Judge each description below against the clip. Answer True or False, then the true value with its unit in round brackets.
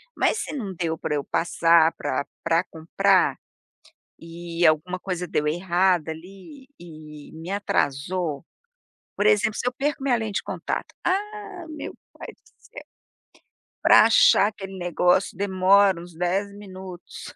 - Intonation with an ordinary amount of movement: True (3.6 semitones)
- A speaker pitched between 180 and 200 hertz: True (185 Hz)